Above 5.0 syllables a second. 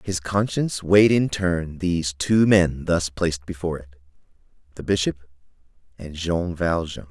No: 4.7 syllables/s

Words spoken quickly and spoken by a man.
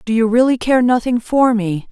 No: fast, 220 wpm; female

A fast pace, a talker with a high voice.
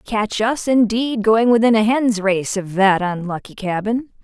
No: average, 170 wpm; high, 215 Hz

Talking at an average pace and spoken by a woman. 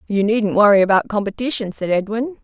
Yes: average, 175 wpm; female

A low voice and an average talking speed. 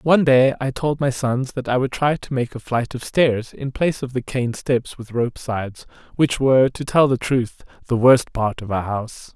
No: low, 125 Hz; fast, 235 wpm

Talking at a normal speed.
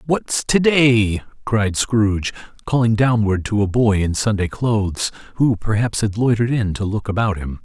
Yes: average, 175 wpm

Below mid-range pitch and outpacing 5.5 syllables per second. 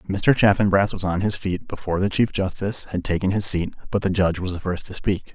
Yes: very low, 95 Hz; 6.0 syllables/s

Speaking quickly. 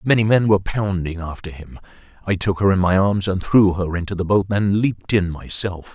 Yes: fast, 220 wpm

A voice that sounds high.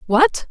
Yes: very high, 290 Hz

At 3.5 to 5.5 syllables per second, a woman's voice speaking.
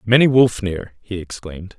No: 4.9 syllables/s; male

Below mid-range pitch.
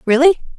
No: very high, 295 Hz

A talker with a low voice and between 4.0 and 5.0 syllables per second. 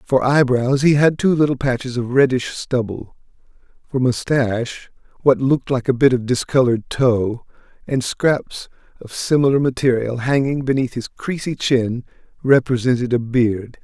Yes: low, 130 Hz; 4.7 syllables/s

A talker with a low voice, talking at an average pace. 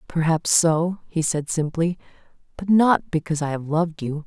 No: medium, 165 Hz; average, 170 wpm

